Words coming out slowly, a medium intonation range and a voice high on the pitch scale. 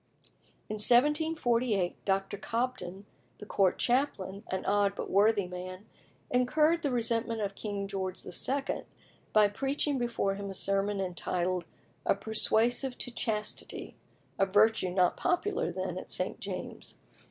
Yes: slow, 130 wpm; average, 4.0 semitones; high, 210 Hz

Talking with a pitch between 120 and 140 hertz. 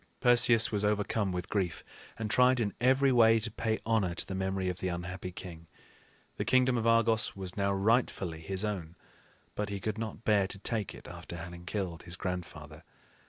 No: low, 100 Hz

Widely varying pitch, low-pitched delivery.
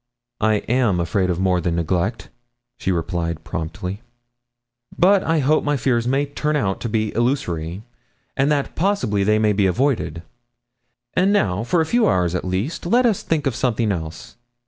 Yes: wide, 8.1 semitones; low, 110 Hz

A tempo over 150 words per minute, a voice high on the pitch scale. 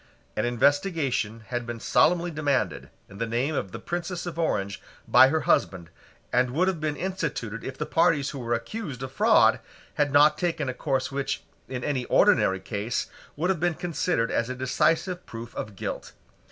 No: average, 180 wpm; low, 135 Hz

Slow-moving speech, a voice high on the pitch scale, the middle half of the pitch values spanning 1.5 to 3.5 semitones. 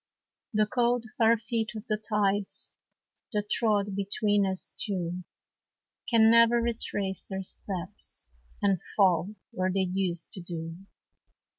Yes: slow, 125 wpm; high, 205 Hz; average, 2.8 semitones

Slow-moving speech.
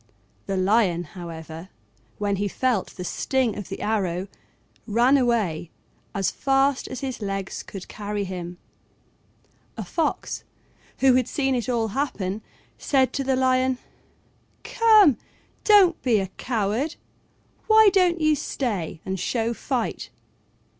Yes: slow, 130 wpm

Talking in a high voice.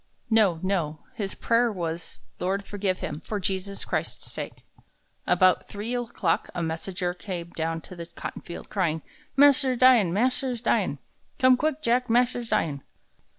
Yes: high, 195 Hz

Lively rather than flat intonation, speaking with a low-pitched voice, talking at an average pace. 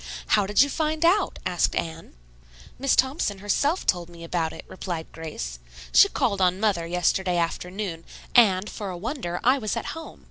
No: wide, 6.5 semitones; high, 190 Hz; average, 175 wpm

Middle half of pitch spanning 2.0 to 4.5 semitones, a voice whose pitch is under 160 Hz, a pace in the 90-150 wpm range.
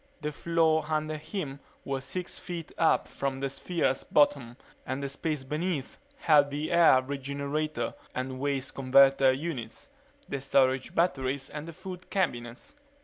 Yes: average, 3.1 semitones; medium, 140 Hz; average, 145 wpm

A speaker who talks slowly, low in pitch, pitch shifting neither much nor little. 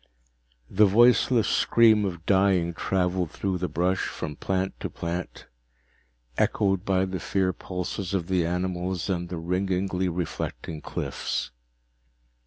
No: slow, 125 wpm; very low, 95 Hz; narrow, 1.7 semitones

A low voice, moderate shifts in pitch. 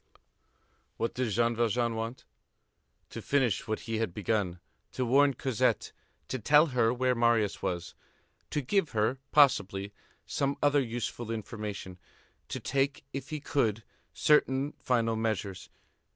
Yes: low, 120 Hz; average, 3.7 semitones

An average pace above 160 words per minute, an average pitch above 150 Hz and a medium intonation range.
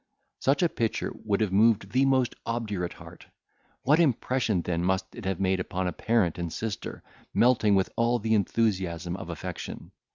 No: average, 170 wpm; low, 105 Hz; average, 4.1 semitones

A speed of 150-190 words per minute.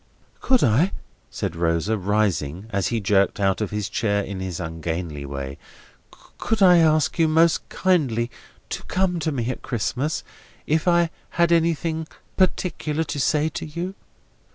Yes: average, 155 wpm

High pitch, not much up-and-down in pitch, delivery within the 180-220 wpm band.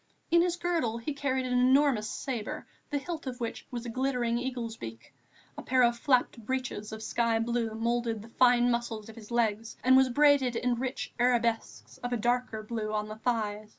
Yes: high, 240 Hz; narrow, 2.3 semitones; average, 195 wpm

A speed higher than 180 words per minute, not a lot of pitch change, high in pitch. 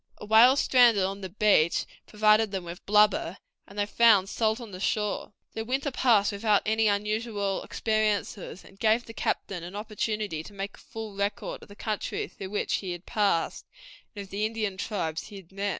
Yes: average, 195 wpm; narrow, 2.0 semitones; high, 210 Hz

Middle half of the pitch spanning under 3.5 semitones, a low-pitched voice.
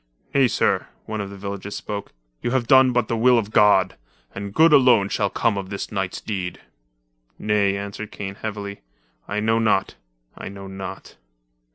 Yes: narrow, 2.4 semitones; low, 100 Hz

